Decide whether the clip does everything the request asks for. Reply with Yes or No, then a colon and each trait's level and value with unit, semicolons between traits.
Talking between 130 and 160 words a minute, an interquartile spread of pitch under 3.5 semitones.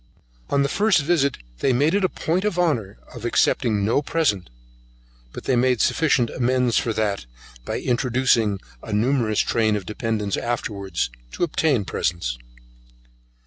No: average, 150 wpm; average, 5.1 semitones